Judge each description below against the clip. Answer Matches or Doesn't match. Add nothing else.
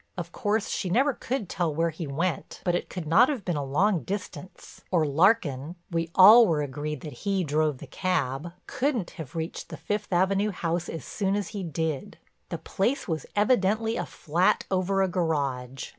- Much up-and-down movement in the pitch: Doesn't match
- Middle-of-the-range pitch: Matches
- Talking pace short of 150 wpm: Doesn't match